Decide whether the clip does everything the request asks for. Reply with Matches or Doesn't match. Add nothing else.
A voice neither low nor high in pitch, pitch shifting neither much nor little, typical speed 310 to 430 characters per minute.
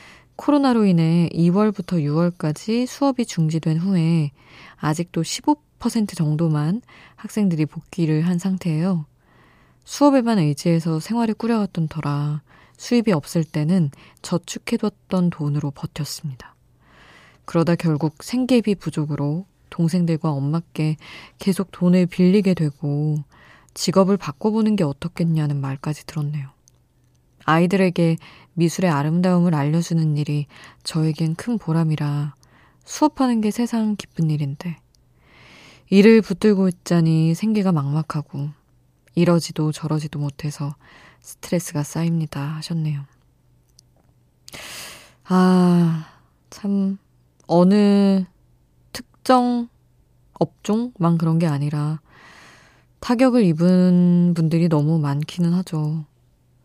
Doesn't match